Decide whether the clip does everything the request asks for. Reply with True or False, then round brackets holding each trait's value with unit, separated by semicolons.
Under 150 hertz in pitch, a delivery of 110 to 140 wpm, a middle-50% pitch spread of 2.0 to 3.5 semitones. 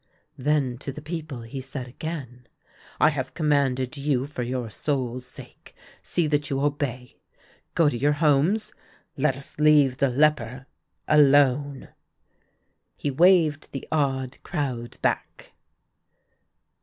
True (140 Hz; 135 wpm; 2.8 semitones)